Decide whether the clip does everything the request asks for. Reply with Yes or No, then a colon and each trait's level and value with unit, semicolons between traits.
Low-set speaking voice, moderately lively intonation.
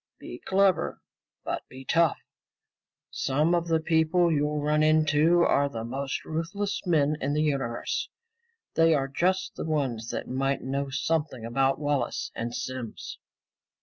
No: medium, 150 Hz; average, 3.4 semitones